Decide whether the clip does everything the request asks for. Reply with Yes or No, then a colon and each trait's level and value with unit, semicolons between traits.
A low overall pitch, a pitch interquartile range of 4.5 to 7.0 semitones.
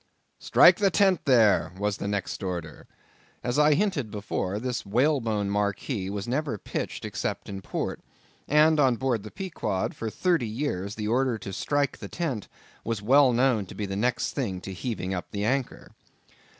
Yes: low, 115 Hz; wide, 5.4 semitones